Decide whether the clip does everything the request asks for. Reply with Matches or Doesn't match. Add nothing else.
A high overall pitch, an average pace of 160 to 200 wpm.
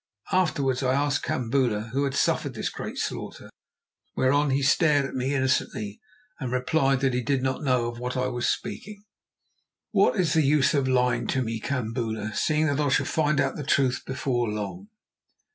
Doesn't match